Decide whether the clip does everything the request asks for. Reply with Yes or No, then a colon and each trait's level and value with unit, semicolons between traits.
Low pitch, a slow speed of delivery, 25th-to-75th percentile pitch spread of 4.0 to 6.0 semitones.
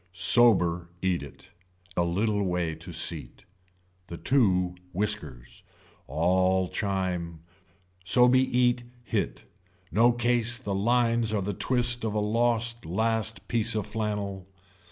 Yes: low, 105 Hz; slow, 125 wpm; average, 4.5 semitones